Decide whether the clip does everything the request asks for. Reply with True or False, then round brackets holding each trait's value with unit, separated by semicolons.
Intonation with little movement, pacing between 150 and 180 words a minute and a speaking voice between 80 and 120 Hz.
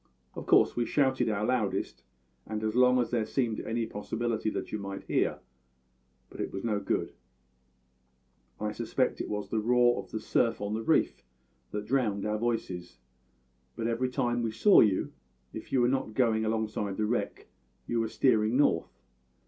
True (2.3 semitones; 175 wpm; 110 Hz)